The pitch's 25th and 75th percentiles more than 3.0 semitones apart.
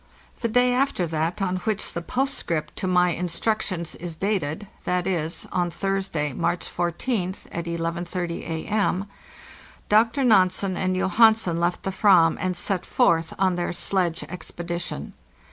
No: average, 2.7 semitones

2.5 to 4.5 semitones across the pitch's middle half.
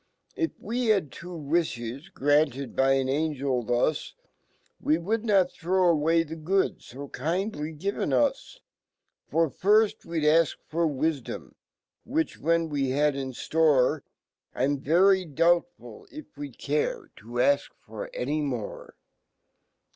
No: average, 5.2 semitones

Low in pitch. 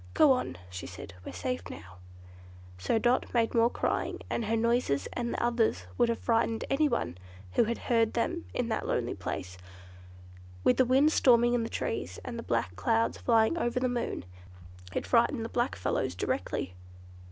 No: high, 230 Hz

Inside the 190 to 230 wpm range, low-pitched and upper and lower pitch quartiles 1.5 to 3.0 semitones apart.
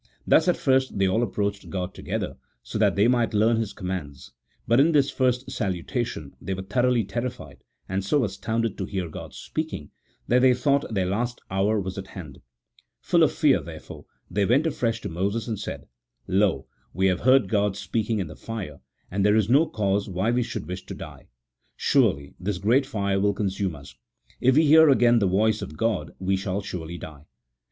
No: average, 200 wpm; low, 105 Hz; average, 4.2 semitones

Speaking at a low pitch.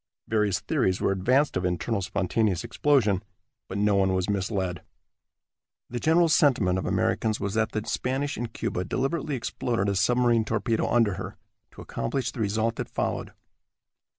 Yes: low, 110 Hz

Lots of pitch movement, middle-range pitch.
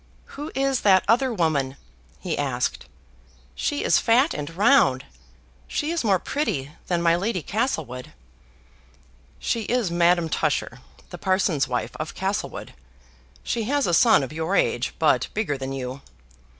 Yes: wide, 8.3 semitones; medium, 180 Hz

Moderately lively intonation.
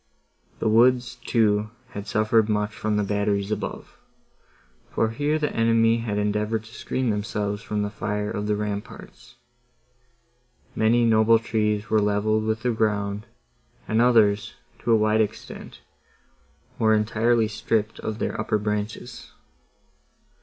No: narrow, 1.6 semitones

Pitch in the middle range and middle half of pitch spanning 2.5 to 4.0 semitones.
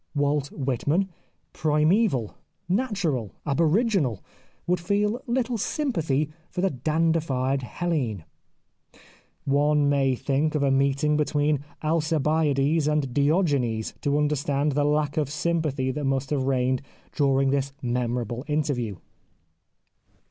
Yes: medium, 145 Hz; average, 3.0 semitones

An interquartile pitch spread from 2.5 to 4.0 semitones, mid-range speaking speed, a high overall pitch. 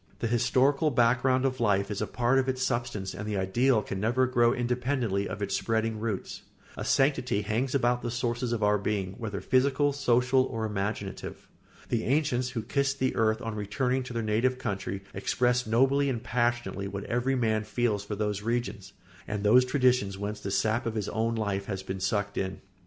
No: average, 3.6 semitones; average, 190 wpm; low, 115 Hz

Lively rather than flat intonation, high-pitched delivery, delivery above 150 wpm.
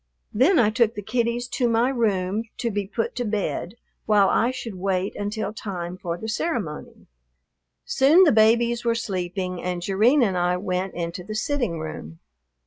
No: average, 4.4 semitones; high, 210 Hz; average, 170 wpm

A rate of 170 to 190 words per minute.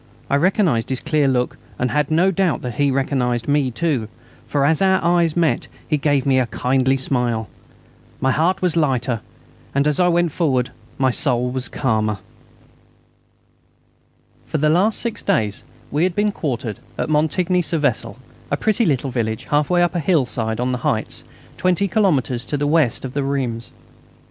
Yes: average, 175 wpm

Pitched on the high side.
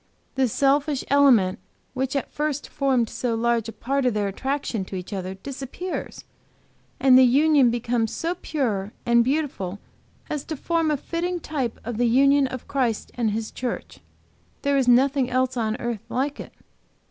Yes: very high, 255 Hz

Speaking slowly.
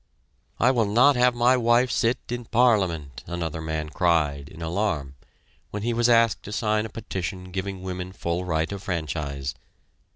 No: average, 165 wpm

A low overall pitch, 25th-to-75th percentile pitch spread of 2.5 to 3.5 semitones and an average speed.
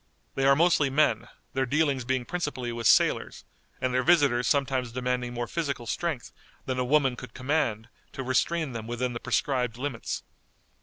Yes: low, 130 Hz; average, 2.9 semitones; average, 165 wpm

